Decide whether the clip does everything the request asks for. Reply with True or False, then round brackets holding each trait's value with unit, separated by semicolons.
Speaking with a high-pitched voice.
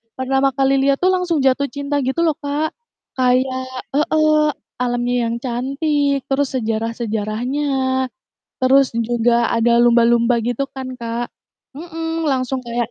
True (260 Hz)